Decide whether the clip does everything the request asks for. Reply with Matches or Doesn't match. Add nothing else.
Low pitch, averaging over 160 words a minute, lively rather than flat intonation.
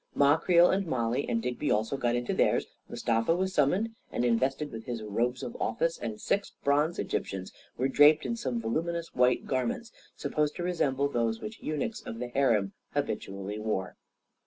Matches